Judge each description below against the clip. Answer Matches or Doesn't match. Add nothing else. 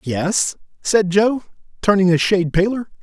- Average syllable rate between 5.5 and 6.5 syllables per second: Doesn't match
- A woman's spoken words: Doesn't match